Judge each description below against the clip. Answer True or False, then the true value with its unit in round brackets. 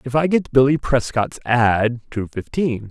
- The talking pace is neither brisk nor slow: True (165 wpm)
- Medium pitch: False (125 Hz)